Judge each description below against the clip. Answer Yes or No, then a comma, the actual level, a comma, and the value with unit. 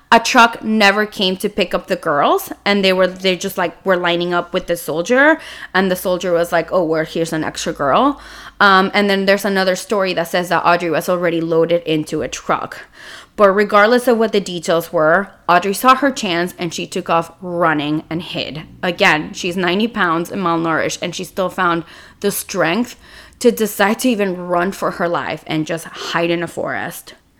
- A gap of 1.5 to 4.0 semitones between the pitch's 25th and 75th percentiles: Yes, average, 3.0 semitones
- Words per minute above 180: Yes, average, 200 wpm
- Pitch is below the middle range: No, medium, 185 Hz